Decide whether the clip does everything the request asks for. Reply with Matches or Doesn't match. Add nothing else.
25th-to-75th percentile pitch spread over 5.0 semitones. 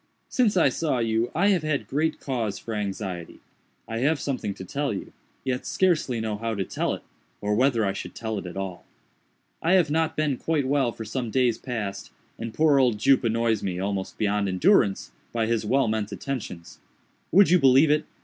Matches